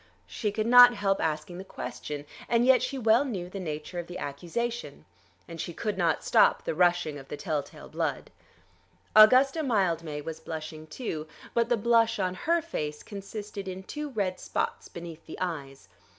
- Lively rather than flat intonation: Yes, wide, 6.3 semitones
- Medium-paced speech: Yes, average, 180 wpm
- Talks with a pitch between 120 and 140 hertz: No, medium, 185 Hz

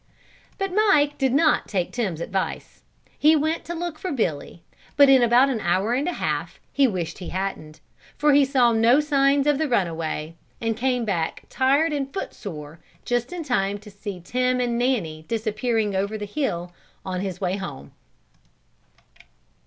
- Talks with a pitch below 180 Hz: No, high, 235 Hz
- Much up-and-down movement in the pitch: Yes, wide, 6.6 semitones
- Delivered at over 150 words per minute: Yes, average, 170 wpm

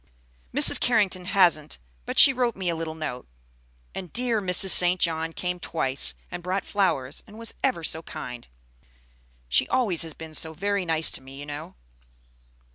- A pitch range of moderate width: Yes, average, 4.0 semitones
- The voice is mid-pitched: Yes, medium, 175 Hz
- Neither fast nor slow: Yes, average, 170 wpm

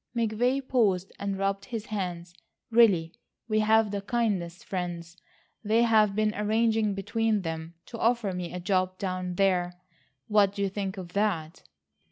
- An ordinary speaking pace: Yes, average, 155 wpm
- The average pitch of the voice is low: No, high, 200 Hz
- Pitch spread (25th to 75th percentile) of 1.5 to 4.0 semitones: Yes, average, 3.2 semitones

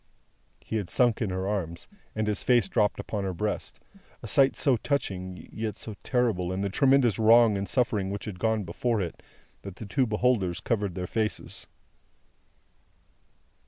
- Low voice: Yes, low, 105 Hz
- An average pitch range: Yes, average, 3.6 semitones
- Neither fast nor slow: Yes, average, 165 wpm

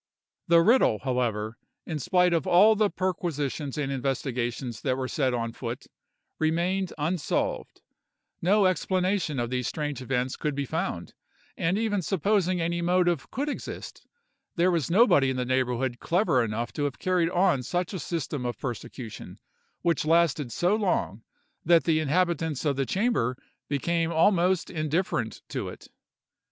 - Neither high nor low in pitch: Yes, medium, 160 Hz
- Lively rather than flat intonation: Yes, wide, 5.7 semitones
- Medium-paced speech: Yes, average, 145 wpm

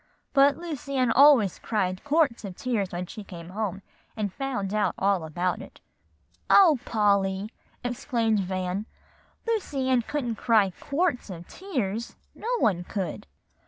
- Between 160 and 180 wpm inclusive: No, slow, 135 wpm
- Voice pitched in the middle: No, high, 220 Hz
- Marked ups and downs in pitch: Yes, wide, 6.1 semitones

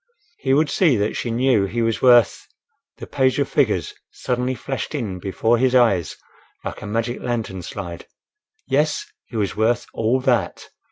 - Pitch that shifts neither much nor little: Yes, average, 3.6 semitones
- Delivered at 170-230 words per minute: No, average, 160 wpm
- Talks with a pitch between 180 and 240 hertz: No, low, 120 Hz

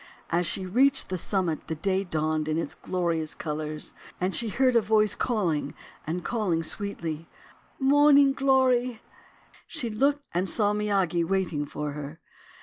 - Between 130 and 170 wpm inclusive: Yes, average, 155 wpm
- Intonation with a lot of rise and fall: Yes, wide, 6.5 semitones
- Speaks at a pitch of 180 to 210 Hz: Yes, high, 190 Hz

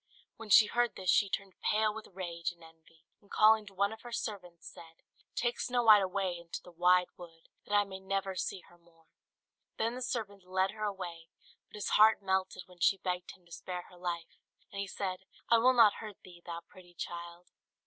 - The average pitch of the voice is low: No, high, 190 Hz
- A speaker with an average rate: No, fast, 210 wpm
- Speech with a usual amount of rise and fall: Yes, average, 3.3 semitones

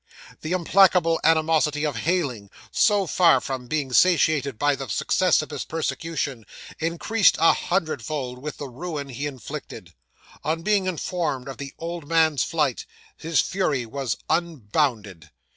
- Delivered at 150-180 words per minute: No, average, 140 wpm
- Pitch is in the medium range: Yes, medium, 155 Hz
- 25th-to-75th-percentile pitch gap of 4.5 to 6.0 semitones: No, average, 3.8 semitones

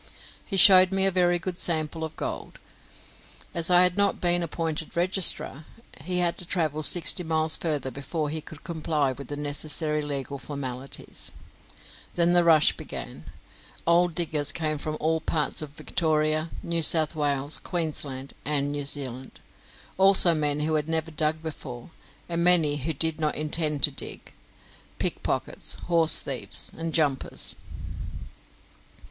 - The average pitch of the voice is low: No, medium, 155 Hz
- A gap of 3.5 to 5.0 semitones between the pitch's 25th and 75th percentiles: No, narrow, 2.5 semitones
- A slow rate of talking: No, average, 150 wpm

